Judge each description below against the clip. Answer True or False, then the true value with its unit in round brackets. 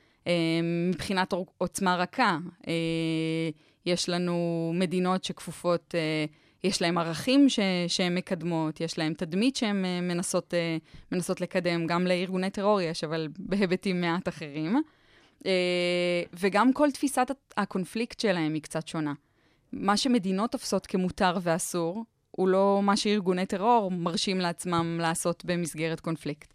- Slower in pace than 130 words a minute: True (115 wpm)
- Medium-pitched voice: True (180 Hz)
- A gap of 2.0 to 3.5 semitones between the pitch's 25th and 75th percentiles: True (2.9 semitones)